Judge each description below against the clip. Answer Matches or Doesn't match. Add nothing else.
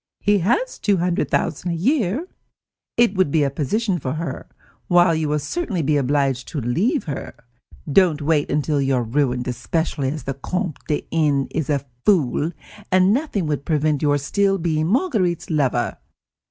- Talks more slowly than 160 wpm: Doesn't match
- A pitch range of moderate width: Matches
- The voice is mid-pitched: Matches